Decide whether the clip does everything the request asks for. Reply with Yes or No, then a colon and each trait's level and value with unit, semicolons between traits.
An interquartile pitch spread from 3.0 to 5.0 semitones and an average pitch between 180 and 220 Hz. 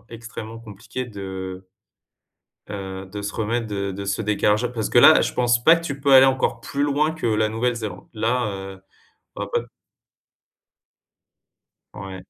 No: average, 3.8 semitones; low, 110 Hz